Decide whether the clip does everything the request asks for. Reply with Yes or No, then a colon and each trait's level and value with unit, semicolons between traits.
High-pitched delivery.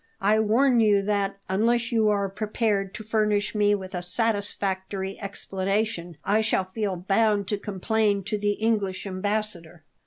Yes: high, 205 Hz